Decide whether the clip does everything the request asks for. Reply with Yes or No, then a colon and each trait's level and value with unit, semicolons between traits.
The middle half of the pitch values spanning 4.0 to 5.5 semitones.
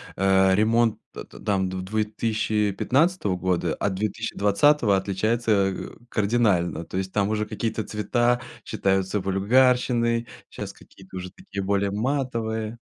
No: average, 3.2 semitones